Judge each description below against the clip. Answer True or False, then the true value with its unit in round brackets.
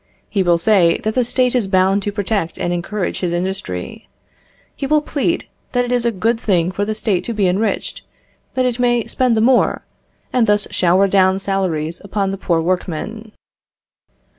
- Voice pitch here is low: False (200 Hz)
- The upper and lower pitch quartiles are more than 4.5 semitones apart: False (4.1 semitones)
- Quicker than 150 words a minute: True (185 wpm)